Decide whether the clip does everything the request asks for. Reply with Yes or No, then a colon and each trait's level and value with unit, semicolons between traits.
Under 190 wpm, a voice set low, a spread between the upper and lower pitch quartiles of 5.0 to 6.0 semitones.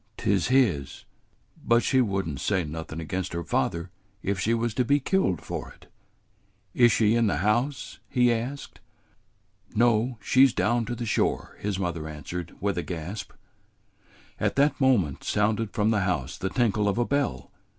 Yes: average, 175 wpm; low, 105 Hz; average, 5.3 semitones